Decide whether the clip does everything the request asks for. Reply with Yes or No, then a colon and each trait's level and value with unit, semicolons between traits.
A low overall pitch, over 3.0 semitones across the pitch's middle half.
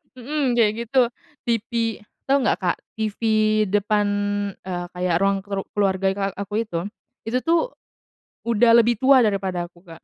No: high, 210 Hz; average, 3.6 semitones